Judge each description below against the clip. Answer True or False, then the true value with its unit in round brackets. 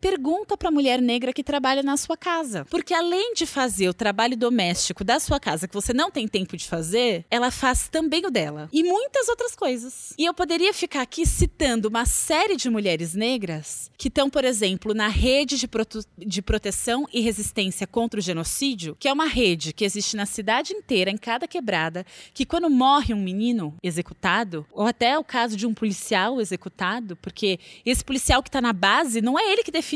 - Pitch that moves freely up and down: True (6.3 semitones)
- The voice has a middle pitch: False (240 Hz)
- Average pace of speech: False (195 wpm)